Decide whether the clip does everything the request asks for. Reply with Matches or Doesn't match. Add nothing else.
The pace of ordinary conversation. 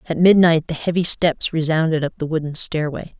Matches